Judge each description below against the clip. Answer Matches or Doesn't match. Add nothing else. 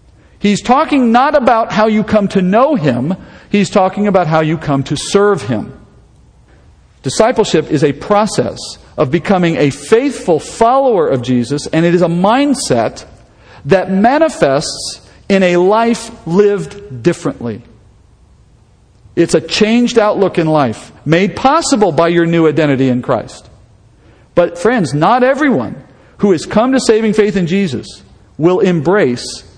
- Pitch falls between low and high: Matches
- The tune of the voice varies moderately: Doesn't match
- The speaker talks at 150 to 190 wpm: Doesn't match